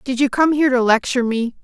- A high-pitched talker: Yes, very high, 255 Hz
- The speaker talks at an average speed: No, fast, 255 wpm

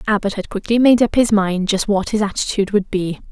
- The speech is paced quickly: Yes, fast, 255 wpm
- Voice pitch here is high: Yes, high, 205 Hz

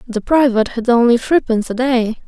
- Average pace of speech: Yes, average, 185 wpm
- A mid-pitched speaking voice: No, high, 240 Hz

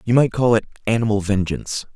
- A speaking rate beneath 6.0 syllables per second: No, 6.3 syllables/s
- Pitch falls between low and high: No, low, 110 Hz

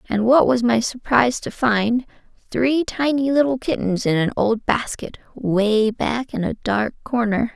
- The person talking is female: Yes, female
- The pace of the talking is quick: No, average, 165 wpm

